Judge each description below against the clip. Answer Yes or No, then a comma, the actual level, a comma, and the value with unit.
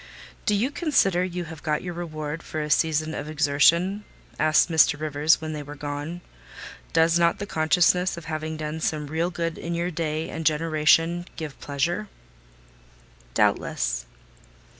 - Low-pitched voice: No, medium, 160 Hz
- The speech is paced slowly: No, average, 155 wpm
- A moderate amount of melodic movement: No, narrow, 2.2 semitones